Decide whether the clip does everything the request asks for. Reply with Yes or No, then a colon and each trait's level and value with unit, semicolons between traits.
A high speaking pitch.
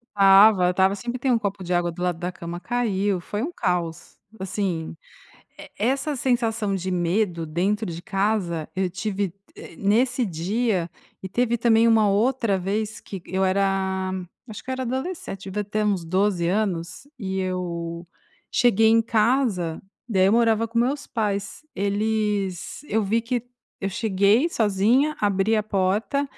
Yes: high, 200 Hz